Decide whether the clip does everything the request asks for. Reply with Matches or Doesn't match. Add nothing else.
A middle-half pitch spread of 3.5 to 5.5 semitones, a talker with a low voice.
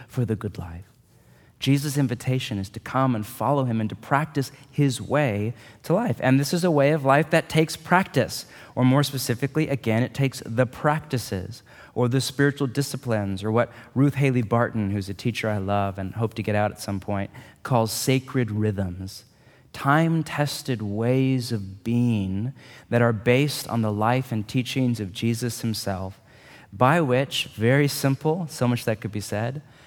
Matches